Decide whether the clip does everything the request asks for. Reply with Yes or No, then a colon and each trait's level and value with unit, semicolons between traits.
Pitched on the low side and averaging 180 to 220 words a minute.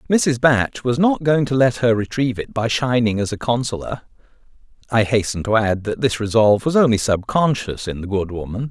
Yes: low, 115 Hz; fast, 205 wpm